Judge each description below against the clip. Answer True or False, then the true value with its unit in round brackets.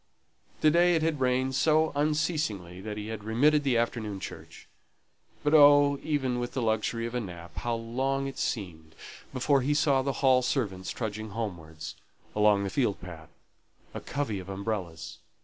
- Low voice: True (120 Hz)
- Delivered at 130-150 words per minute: False (165 wpm)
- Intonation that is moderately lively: False (5.8 semitones)